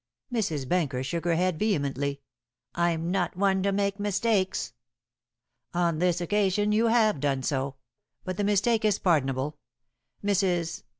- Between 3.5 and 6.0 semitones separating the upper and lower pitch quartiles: Yes, average, 4.7 semitones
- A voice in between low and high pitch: Yes, medium, 180 Hz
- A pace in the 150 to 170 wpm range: No, average, 140 wpm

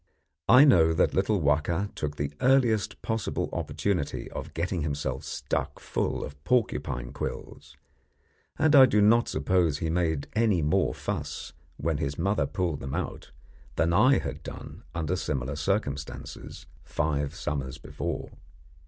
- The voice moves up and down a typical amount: No, wide, 6.0 semitones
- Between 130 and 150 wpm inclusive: Yes, average, 140 wpm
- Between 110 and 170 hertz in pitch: No, very low, 80 Hz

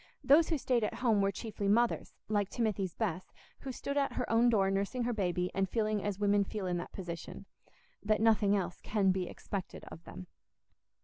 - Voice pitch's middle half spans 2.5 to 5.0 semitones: Yes, average, 3.2 semitones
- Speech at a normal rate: Yes, average, 190 wpm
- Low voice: No, high, 205 Hz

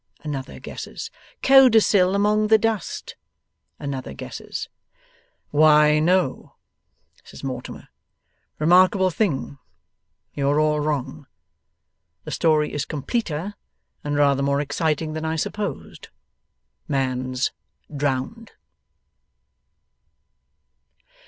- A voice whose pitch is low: No, medium, 150 Hz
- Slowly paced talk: Yes, slow, 85 wpm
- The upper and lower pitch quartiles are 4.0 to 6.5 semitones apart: Yes, average, 4.9 semitones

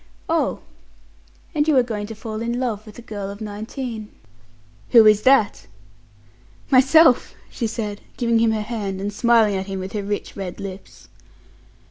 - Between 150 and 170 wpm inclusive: Yes, average, 165 wpm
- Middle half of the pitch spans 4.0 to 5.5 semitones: No, narrow, 2.6 semitones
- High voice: Yes, high, 215 Hz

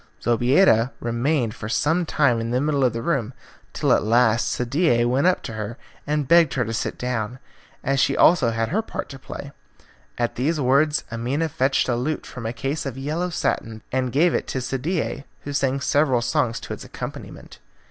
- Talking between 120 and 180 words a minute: No, average, 195 wpm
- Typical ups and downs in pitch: Yes, average, 3.9 semitones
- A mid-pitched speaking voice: No, low, 130 Hz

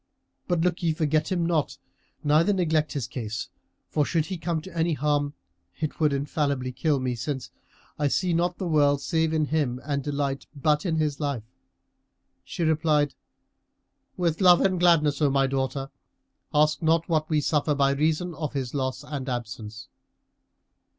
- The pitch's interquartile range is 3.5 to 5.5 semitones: No, average, 2.7 semitones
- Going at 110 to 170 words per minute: Yes, average, 165 wpm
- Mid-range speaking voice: Yes, medium, 150 Hz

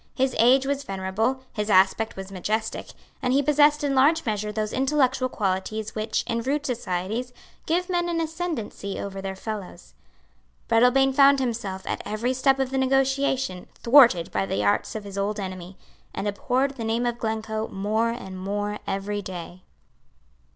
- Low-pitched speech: No, high, 225 Hz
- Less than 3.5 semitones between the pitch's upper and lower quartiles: No, average, 5.2 semitones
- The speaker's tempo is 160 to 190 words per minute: Yes, average, 165 wpm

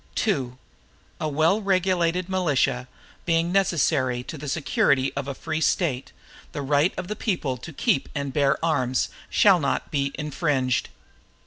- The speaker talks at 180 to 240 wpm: No, average, 145 wpm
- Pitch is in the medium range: Yes, medium, 150 Hz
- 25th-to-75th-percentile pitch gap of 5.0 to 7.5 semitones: No, average, 4.3 semitones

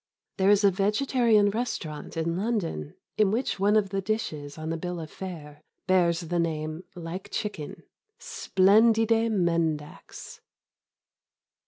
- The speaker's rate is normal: No, slow, 130 wpm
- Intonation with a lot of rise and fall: No, average, 4.6 semitones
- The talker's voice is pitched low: No, medium, 185 Hz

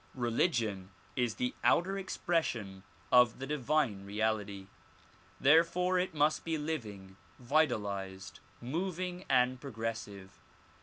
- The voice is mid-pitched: No, low, 125 Hz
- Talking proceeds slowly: Yes, slow, 100 wpm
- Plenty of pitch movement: Yes, wide, 7.5 semitones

